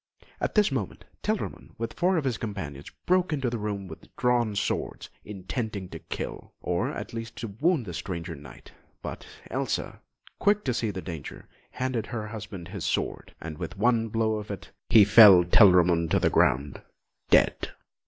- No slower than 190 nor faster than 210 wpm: No, average, 175 wpm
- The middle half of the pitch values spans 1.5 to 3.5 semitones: No, average, 4.9 semitones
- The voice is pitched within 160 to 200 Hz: No, low, 105 Hz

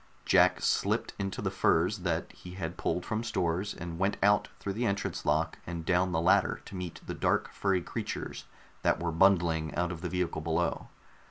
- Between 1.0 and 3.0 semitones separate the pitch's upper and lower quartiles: Yes, average, 2.7 semitones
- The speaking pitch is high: No, very low, 90 Hz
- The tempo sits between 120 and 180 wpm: No, average, 190 wpm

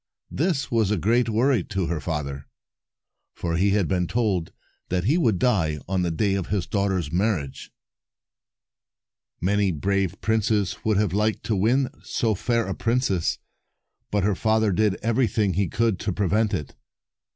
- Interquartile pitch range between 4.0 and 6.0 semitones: No, average, 3.5 semitones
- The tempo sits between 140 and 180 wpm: Yes, average, 160 wpm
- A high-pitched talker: No, low, 100 Hz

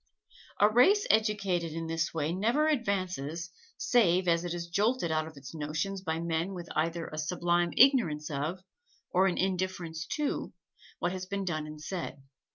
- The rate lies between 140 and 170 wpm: Yes, average, 165 wpm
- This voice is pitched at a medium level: Yes, medium, 175 Hz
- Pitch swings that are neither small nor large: Yes, average, 3.4 semitones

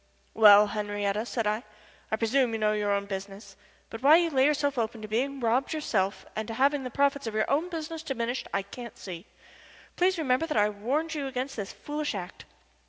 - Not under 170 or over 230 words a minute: Yes, fast, 205 wpm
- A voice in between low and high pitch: No, high, 235 Hz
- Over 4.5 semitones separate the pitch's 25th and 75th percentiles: Yes, average, 5.2 semitones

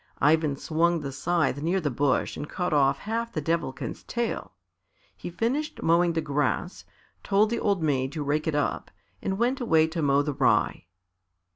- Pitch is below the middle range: No, medium, 160 Hz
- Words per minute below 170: No, average, 175 wpm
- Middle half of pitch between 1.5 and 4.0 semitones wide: No, average, 4.8 semitones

